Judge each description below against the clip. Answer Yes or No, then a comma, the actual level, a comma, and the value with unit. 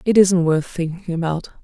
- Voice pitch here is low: No, medium, 175 Hz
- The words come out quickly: No, average, 185 wpm